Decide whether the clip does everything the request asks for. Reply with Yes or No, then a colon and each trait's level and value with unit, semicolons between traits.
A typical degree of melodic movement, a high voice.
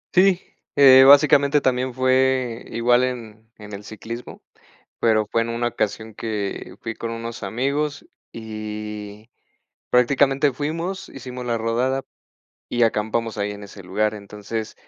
No: average, 3.5 semitones; low, 115 Hz